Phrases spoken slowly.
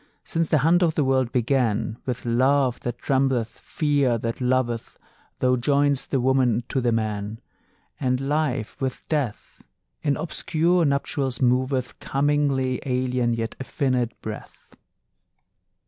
Yes: slow, 130 wpm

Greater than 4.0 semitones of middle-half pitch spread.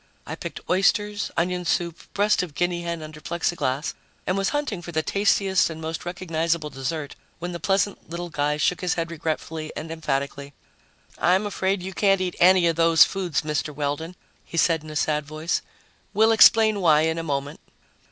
No: average, 3.1 semitones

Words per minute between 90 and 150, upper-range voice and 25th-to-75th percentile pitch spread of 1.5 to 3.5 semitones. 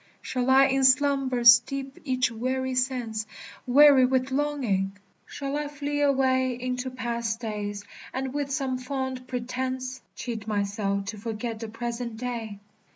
Yes: average, 140 wpm; very high, 255 Hz; narrow, 2.6 semitones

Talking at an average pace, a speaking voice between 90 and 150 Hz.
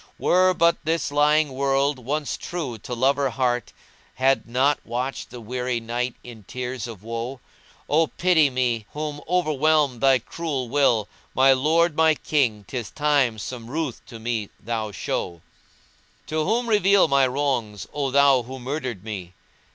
Yes: average, 160 wpm; low, 135 Hz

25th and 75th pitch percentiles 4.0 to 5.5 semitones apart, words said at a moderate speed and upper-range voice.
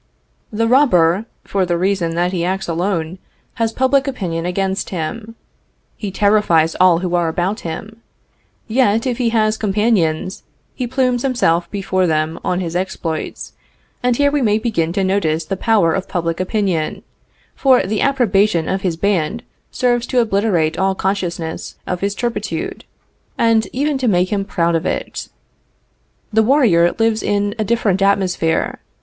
Yes: average, 4.7 semitones; average, 155 wpm; high, 195 Hz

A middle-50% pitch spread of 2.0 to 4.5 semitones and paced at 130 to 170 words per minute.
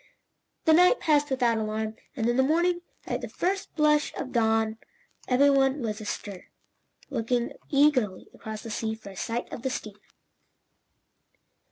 No: average, 4.9 semitones; average, 155 wpm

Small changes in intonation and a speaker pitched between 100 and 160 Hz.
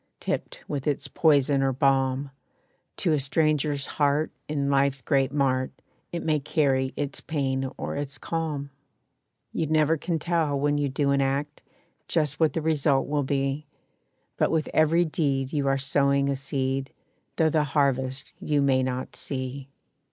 Yes: narrow, 2.0 semitones; medium, 140 Hz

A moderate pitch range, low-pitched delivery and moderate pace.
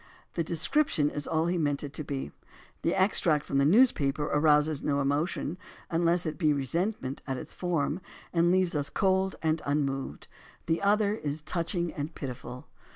No: average, 3.6 semitones; medium, 155 Hz; average, 170 wpm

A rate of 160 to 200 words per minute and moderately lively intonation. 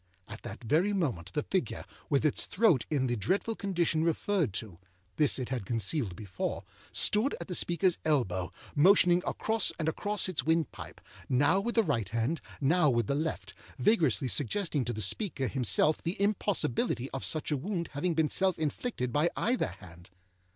No: average, 170 wpm; wide, 7.2 semitones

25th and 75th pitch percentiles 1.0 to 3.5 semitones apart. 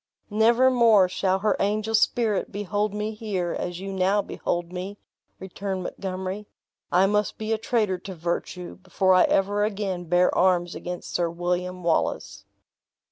Yes: narrow, 2.6 semitones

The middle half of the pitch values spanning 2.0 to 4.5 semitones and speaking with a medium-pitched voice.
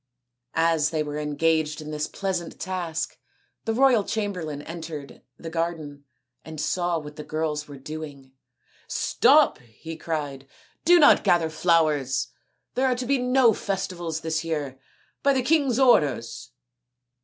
Yes: average, 4.1 semitones; medium, 160 Hz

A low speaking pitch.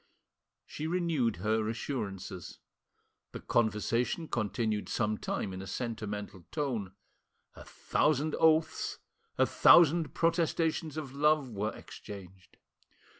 Yes: low, 120 Hz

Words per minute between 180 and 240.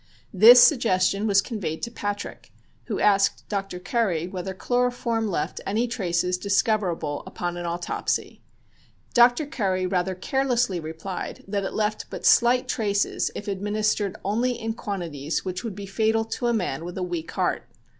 No: average, 155 wpm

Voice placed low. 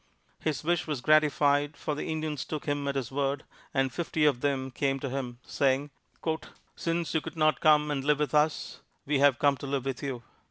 No: medium, 145 Hz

